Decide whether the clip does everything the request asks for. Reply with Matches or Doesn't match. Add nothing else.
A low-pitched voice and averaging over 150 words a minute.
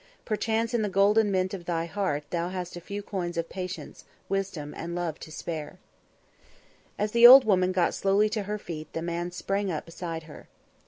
Doesn't match